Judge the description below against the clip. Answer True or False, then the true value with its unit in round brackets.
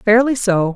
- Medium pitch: False (215 Hz)